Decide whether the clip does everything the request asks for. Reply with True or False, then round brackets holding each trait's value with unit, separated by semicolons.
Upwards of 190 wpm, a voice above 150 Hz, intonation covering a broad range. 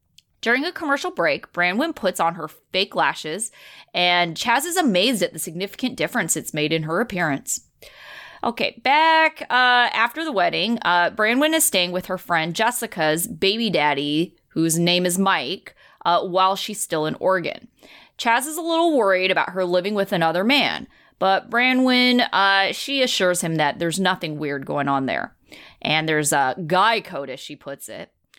False (175 wpm; 185 Hz; 6.8 semitones)